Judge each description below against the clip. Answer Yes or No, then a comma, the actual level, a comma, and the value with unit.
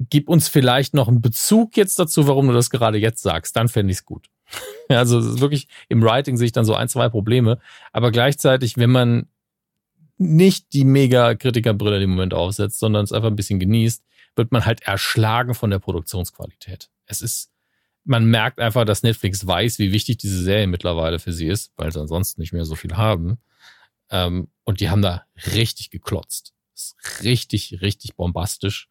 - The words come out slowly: No, average, 185 wpm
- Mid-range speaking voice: No, low, 115 Hz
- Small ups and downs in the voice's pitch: No, average, 3.7 semitones